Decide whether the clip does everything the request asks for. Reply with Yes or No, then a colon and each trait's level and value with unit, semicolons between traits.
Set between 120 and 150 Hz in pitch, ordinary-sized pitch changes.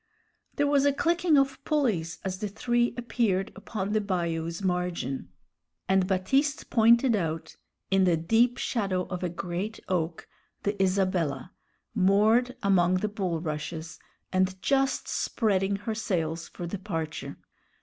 No: high, 190 Hz; average, 4.8 semitones